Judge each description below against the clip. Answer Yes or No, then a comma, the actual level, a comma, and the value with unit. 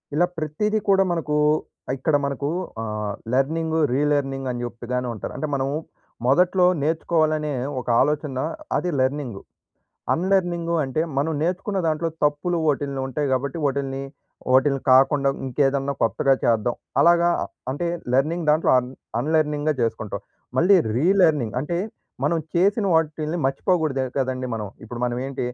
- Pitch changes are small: No, average, 3.7 semitones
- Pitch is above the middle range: No, medium, 145 Hz